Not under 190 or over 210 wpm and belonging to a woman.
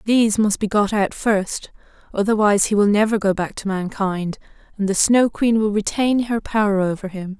Yes: average, 195 wpm; female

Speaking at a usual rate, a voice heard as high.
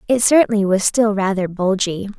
Yes: average, 165 wpm; high, 205 Hz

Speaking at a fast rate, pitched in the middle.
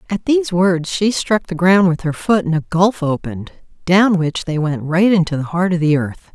Yes: fast, 235 wpm; medium, 175 Hz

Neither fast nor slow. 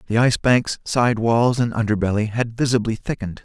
Yes: average, 175 wpm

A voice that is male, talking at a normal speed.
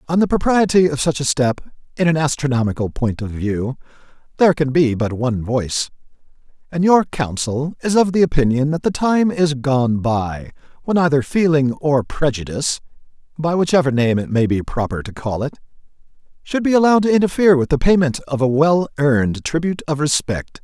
Yes: male; average, 180 wpm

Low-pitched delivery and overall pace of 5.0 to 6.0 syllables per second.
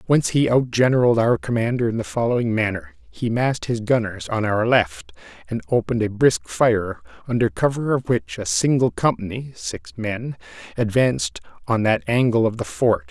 Yes: low, 120 Hz; 5.2 syllables/s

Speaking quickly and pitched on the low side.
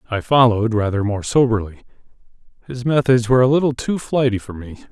No: average, 160 wpm; low, 120 Hz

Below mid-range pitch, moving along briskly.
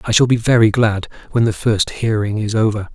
Yes: low, 110 Hz; fast, 225 wpm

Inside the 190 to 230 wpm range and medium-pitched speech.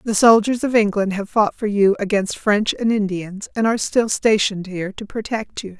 No: fast, 205 wpm; high, 210 Hz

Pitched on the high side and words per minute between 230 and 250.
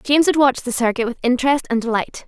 Yes: very high, 255 Hz; fast, 235 wpm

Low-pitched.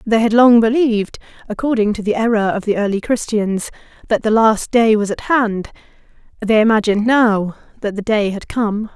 No: high, 220 Hz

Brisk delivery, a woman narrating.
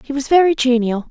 Yes: fast, 220 wpm; female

